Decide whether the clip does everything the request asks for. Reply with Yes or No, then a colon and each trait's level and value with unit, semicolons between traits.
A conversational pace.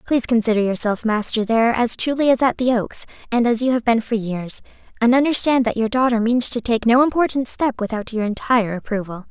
No: fast, 215 wpm